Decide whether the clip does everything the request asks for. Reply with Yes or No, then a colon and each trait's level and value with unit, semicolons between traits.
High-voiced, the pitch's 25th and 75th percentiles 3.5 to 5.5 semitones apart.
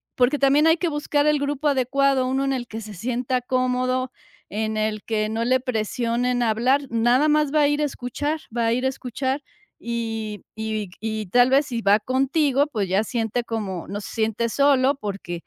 Yes: very high, 250 Hz; average, 3.8 semitones